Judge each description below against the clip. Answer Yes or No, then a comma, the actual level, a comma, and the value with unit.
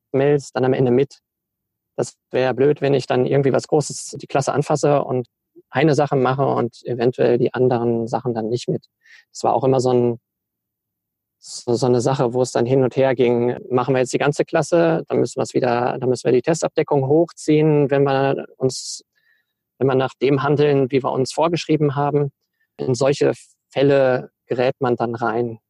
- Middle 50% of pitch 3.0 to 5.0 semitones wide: No, narrow, 2.6 semitones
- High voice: No, low, 135 Hz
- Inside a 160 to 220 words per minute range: Yes, average, 185 wpm